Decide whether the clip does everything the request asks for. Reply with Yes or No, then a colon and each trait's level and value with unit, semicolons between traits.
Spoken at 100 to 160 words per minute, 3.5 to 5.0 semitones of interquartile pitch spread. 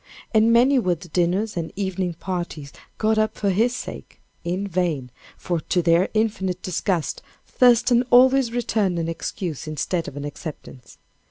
Yes: average, 155 wpm; average, 4.6 semitones